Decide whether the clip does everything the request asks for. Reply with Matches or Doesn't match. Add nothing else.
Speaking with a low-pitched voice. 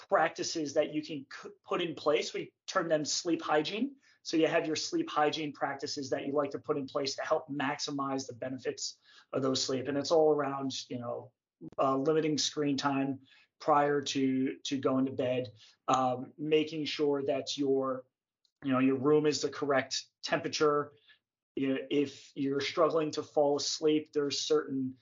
Doesn't match